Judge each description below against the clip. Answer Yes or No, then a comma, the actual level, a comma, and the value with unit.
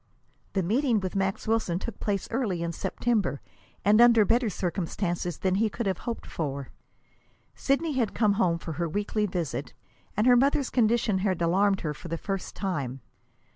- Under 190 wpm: Yes, average, 175 wpm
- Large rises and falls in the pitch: No, average, 4.7 semitones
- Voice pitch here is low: No, high, 195 Hz